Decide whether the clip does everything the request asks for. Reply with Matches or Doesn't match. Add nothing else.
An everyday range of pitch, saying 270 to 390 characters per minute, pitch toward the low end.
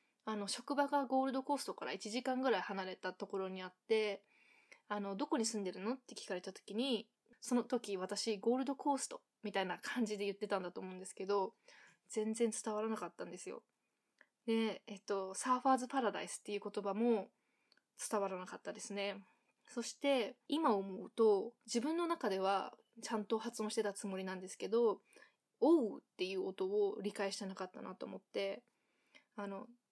Doesn't match